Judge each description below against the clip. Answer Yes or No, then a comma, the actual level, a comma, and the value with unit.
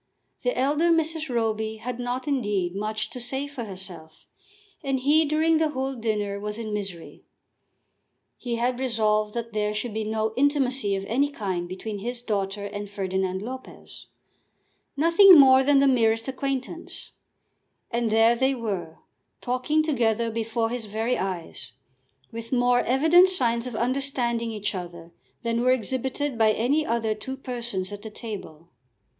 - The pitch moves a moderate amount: Yes, average, 4.0 semitones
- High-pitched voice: Yes, high, 235 Hz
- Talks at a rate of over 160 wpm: No, average, 150 wpm